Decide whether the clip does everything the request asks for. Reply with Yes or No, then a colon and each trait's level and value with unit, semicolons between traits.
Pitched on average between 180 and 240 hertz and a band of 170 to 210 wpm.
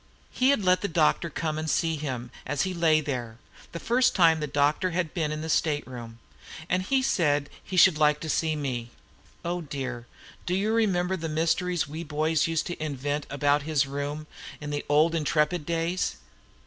No: medium, 155 Hz; average, 190 wpm